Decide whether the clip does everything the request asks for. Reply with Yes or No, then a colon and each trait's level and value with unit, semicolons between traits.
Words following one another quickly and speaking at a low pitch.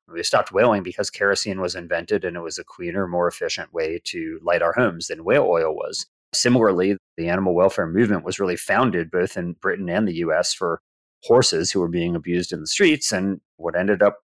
Yes: fast, 210 wpm; low, 100 Hz